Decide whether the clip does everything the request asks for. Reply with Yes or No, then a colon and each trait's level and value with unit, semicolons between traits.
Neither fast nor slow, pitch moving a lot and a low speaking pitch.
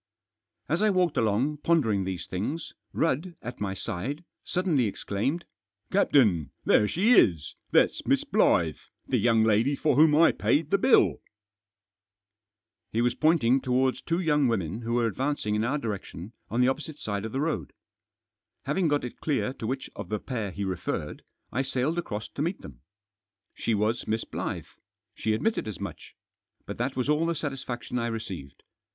Yes: average, 175 wpm; wide, 6.1 semitones; low, 120 Hz